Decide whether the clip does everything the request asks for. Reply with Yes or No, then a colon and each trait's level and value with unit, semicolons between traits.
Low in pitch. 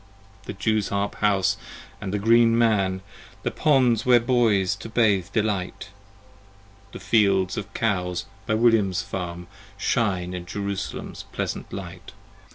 Yes: low, 100 Hz